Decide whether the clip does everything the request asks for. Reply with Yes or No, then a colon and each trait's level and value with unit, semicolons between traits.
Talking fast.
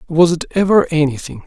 No: average, 165 wpm